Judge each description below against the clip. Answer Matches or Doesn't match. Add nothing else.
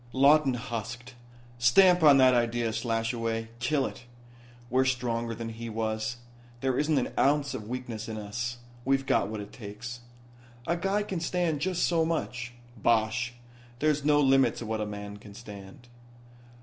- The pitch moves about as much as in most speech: Matches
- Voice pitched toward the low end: Matches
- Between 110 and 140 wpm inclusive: Doesn't match